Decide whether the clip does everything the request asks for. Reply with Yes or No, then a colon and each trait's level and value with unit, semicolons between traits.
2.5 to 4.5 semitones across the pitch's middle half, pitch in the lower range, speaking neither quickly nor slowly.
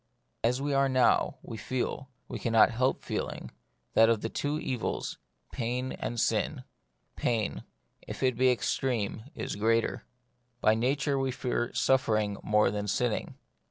Yes: average, 2.8 semitones; low, 120 Hz; average, 155 wpm